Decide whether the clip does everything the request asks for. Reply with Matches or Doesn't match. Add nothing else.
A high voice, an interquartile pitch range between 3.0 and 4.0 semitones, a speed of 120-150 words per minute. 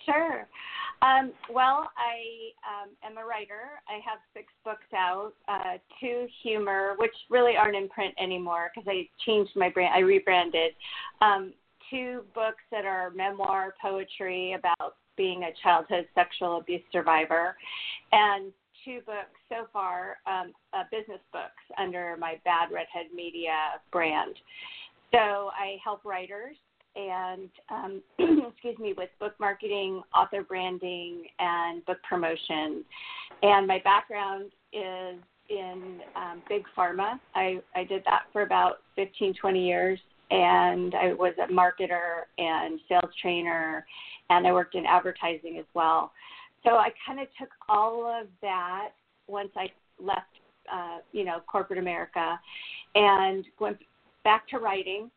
Matches